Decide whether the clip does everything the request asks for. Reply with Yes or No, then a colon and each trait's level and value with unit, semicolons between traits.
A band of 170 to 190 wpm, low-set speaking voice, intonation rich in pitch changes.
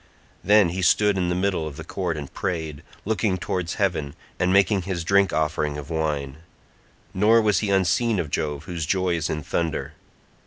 No: average, 185 wpm; very low, 90 Hz; average, 4.0 semitones